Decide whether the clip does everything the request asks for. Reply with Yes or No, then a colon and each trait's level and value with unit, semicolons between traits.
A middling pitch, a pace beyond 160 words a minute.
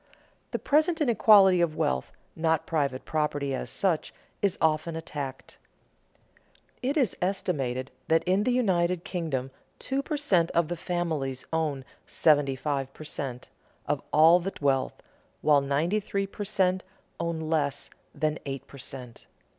No: medium, 160 Hz; average, 145 wpm